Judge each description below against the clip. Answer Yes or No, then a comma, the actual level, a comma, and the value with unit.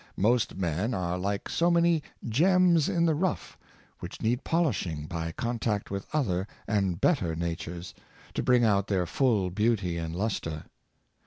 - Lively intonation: Yes, wide, 6.9 semitones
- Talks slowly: No, average, 150 wpm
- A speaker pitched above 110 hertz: No, low, 105 Hz